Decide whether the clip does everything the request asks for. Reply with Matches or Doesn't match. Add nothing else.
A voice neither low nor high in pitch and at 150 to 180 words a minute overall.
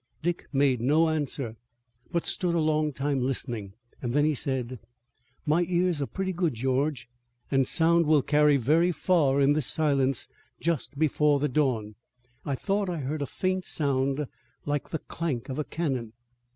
Matches